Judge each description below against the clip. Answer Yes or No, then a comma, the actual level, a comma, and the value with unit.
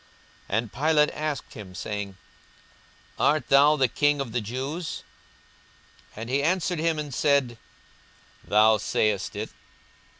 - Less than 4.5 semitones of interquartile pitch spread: No, average, 5.3 semitones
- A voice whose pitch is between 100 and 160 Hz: Yes, low, 135 Hz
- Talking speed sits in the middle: No, slow, 130 wpm